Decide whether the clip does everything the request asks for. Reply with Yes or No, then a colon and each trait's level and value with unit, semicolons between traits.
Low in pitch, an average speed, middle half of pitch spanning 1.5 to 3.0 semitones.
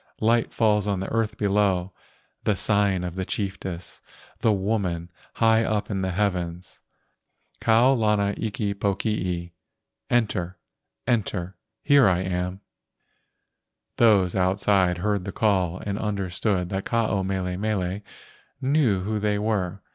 No: low, 100 Hz; slow, 130 wpm; narrow, 2.6 semitones